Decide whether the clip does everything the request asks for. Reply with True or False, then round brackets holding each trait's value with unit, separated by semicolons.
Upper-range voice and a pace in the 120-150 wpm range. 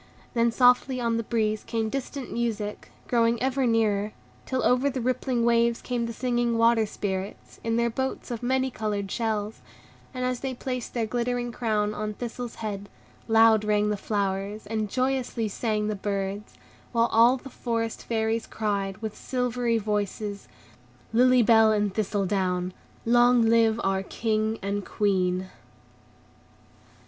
True (225 Hz; 145 wpm)